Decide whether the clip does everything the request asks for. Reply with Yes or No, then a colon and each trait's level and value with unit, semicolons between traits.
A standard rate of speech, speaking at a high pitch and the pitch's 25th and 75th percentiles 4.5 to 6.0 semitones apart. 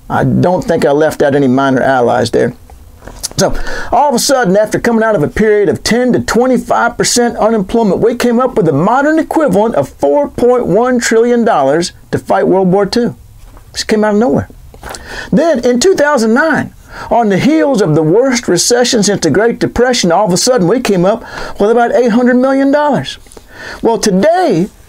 Yes: average, 195 wpm; high, 225 Hz; wide, 5.5 semitones